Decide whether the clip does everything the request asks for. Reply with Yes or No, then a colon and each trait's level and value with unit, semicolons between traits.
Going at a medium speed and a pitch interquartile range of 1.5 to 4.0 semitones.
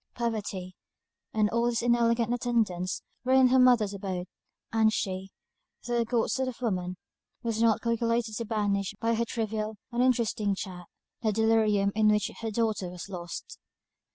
Yes: average, 160 wpm; average, 2.8 semitones